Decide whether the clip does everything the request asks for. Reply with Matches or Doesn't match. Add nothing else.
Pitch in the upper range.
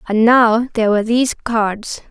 Matches